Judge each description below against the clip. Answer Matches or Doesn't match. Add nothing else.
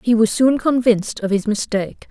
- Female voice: Matches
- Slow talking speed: Doesn't match